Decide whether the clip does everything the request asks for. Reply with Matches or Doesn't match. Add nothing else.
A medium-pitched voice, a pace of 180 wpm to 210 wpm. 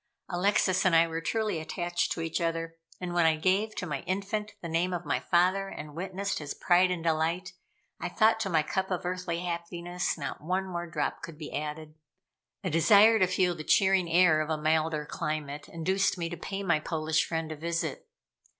Matches